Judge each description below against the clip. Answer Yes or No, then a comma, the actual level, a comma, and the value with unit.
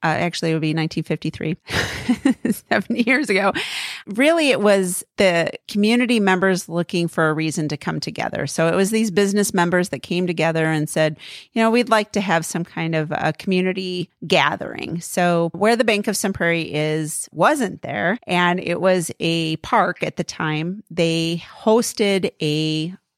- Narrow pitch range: No, average, 4.3 semitones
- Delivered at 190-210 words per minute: No, average, 170 wpm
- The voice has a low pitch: No, medium, 175 Hz